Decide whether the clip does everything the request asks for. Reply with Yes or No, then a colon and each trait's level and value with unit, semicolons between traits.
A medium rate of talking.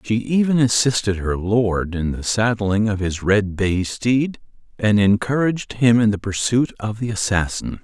Yes: average, 170 wpm